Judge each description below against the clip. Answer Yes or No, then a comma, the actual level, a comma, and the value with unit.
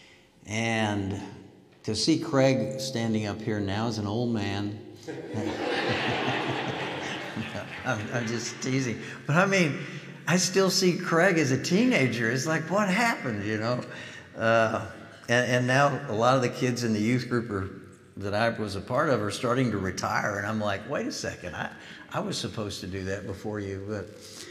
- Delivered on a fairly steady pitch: No, average, 4.1 semitones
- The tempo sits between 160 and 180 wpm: Yes, average, 175 wpm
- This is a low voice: Yes, low, 115 Hz